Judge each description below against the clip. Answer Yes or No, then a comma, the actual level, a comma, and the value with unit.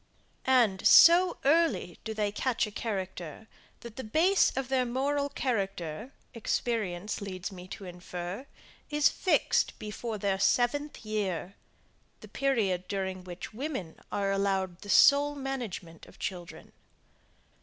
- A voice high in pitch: Yes, high, 210 Hz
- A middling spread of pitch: No, wide, 5.9 semitones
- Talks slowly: Yes, slow, 130 wpm